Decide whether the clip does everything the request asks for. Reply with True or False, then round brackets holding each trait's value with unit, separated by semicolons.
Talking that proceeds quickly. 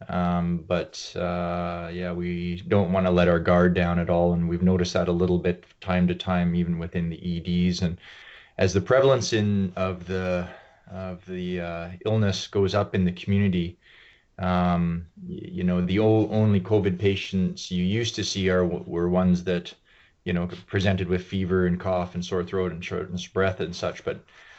False (190 wpm)